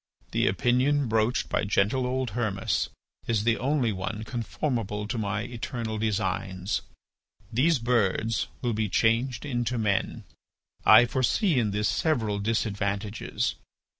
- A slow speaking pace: Yes, slow, 125 wpm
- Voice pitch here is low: Yes, low, 110 Hz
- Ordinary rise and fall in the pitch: Yes, average, 3.0 semitones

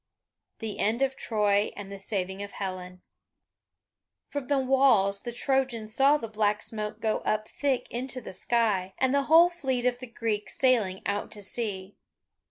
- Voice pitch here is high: Yes, high, 220 Hz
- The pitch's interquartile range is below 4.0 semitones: No, average, 4.4 semitones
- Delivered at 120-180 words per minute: Yes, average, 170 wpm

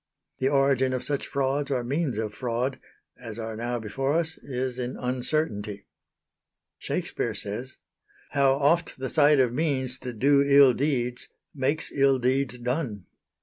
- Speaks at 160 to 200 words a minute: No, average, 145 wpm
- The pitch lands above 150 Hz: No, low, 130 Hz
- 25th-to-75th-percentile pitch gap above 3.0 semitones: No, narrow, 2.4 semitones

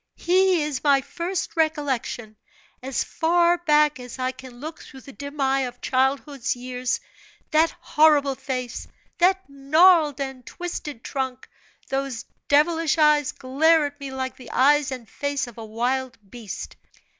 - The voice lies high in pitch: Yes, very high, 275 Hz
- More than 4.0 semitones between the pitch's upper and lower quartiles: No, average, 3.2 semitones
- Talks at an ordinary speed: Yes, average, 145 wpm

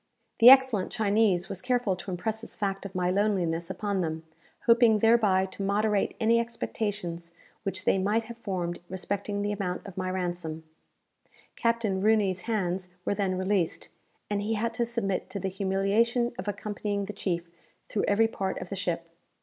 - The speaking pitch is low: No, high, 200 Hz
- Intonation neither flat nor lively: Yes, average, 3.0 semitones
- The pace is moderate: Yes, average, 170 wpm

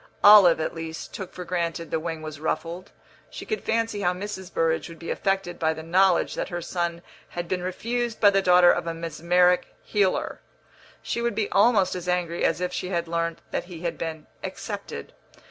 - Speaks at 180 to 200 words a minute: Yes, average, 195 wpm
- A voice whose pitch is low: No, medium, 175 Hz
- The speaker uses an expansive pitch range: No, narrow, 2.4 semitones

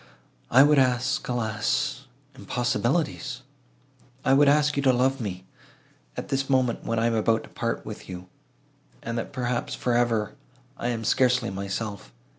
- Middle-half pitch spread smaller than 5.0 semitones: Yes, average, 2.9 semitones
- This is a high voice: No, low, 120 Hz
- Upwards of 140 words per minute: Yes, average, 155 wpm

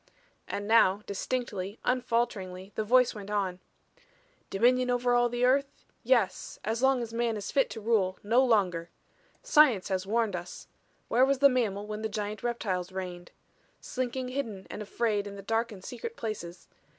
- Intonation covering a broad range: No, average, 3.9 semitones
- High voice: Yes, high, 220 Hz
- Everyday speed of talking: Yes, average, 165 wpm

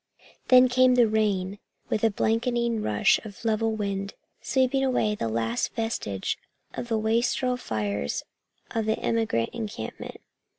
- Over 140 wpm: No, slow, 135 wpm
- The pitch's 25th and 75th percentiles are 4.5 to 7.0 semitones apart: No, average, 3.3 semitones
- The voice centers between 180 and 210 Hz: No, high, 220 Hz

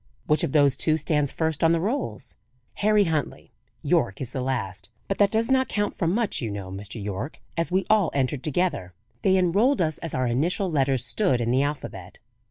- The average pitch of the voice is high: No, medium, 150 Hz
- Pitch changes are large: Yes, wide, 7.1 semitones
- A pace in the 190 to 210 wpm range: Yes, average, 200 wpm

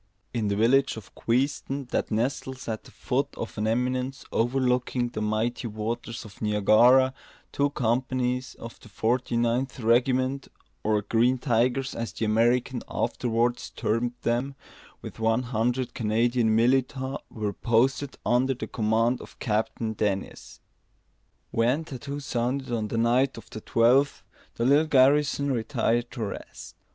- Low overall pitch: Yes, low, 120 Hz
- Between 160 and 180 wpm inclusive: No, average, 140 wpm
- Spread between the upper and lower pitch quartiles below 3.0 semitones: Yes, narrow, 2.6 semitones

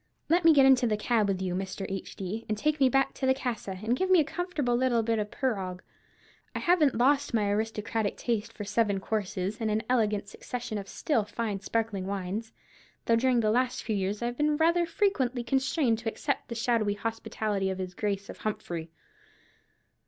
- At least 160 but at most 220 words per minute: Yes, average, 195 wpm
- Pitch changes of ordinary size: Yes, average, 4.1 semitones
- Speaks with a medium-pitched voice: No, high, 225 Hz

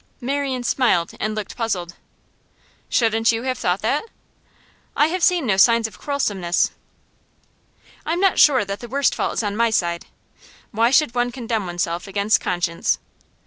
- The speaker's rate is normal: Yes, average, 155 wpm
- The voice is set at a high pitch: Yes, high, 225 Hz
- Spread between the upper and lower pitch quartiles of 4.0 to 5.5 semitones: Yes, average, 4.8 semitones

